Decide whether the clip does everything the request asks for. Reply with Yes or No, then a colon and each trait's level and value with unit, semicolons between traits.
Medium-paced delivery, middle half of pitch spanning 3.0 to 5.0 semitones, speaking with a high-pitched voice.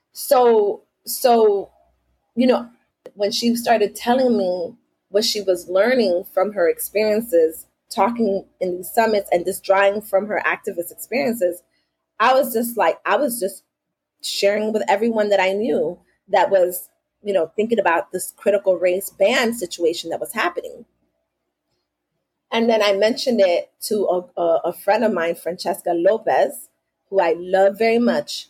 Yes: average, 150 wpm; average, 4.7 semitones; high, 195 Hz